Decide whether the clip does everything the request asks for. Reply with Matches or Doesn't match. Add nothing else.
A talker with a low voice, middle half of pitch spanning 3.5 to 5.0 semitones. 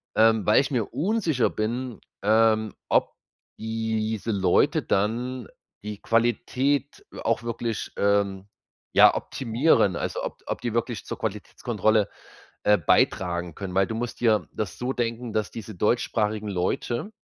Doesn't match